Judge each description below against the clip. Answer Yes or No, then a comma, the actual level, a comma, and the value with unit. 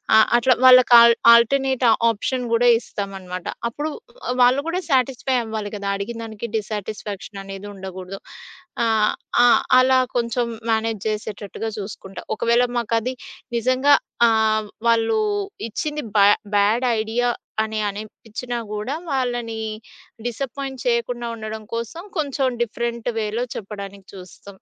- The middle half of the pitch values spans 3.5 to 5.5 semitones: No, average, 2.9 semitones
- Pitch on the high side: Yes, high, 230 Hz